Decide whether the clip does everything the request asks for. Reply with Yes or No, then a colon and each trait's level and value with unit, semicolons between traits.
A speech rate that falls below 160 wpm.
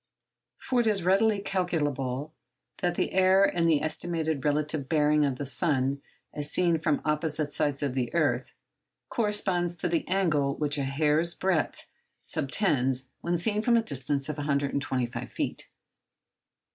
Yes: average, 145 wpm